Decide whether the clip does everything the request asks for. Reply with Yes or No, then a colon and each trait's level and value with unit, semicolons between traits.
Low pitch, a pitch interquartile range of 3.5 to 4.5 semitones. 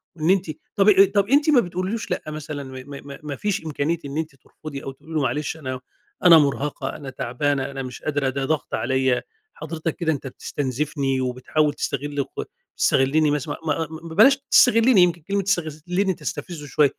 No: medium, 150 Hz; average, 4.1 semitones